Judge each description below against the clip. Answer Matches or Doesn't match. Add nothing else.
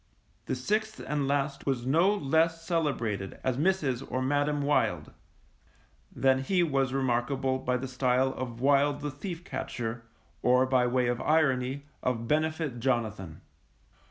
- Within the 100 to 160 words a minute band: Matches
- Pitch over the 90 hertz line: Matches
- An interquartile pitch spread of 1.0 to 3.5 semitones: Matches